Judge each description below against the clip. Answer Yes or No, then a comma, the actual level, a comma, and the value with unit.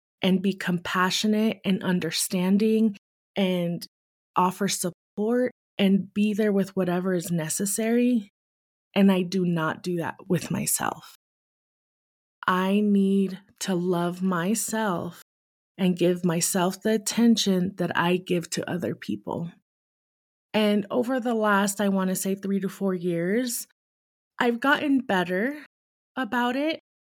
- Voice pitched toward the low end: No, high, 195 Hz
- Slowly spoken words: Yes, slow, 120 wpm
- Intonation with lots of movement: No, average, 3.0 semitones